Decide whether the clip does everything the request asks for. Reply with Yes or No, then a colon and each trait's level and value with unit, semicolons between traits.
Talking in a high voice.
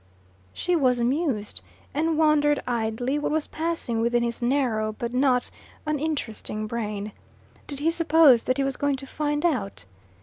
Yes: very high, 265 Hz